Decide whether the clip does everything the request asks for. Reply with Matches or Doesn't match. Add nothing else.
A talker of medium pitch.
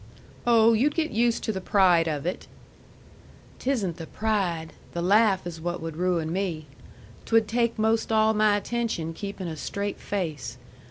Doesn't match